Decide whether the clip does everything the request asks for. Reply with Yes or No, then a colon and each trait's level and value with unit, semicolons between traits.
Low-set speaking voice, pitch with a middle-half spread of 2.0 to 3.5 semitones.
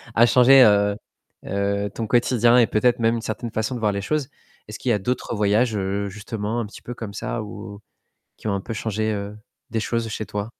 Yes: low, 110 Hz; narrow, 2.6 semitones